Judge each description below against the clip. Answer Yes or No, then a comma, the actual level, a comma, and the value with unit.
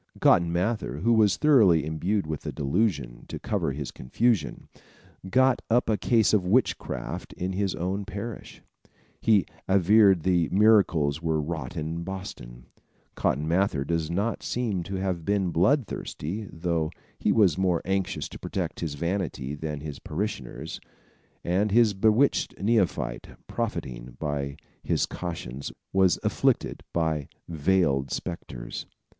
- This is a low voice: Yes, very low, 90 Hz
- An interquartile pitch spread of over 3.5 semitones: Yes, average, 4.8 semitones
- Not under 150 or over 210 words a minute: No, slow, 135 wpm